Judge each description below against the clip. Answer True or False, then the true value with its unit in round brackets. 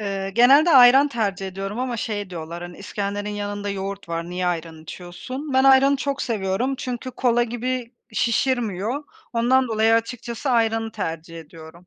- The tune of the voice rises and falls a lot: False (4.8 semitones)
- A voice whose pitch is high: True (220 Hz)